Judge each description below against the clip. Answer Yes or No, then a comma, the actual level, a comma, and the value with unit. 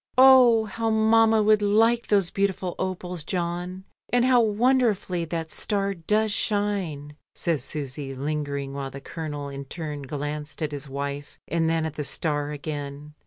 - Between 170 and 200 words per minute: No, average, 155 wpm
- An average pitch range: No, wide, 6.1 semitones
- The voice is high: No, medium, 170 Hz